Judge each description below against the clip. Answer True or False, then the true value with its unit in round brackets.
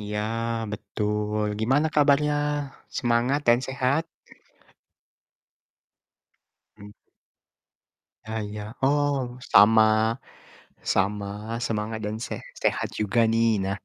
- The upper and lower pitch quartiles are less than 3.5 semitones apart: True (2.8 semitones)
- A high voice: False (110 Hz)